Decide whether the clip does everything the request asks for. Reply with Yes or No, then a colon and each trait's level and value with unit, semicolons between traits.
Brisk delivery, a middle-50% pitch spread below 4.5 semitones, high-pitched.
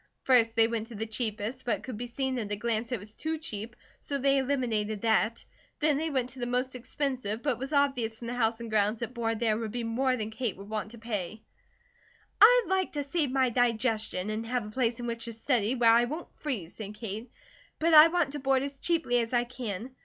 Yes: fast, 245 wpm; average, 3.2 semitones; high, 240 Hz